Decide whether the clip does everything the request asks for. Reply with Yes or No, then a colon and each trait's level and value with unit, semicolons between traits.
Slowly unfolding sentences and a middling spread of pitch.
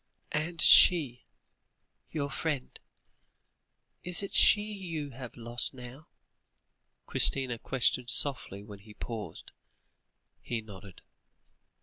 Yes: slow, 95 wpm; average, 5.0 semitones